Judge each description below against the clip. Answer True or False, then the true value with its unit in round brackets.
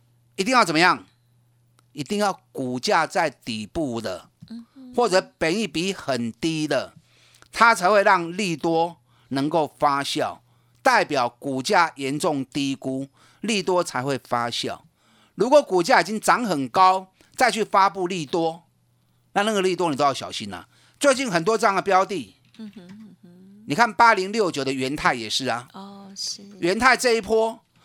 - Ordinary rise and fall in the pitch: False (7.6 semitones)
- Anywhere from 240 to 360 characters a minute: False (220 characters per minute)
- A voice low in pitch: False (180 Hz)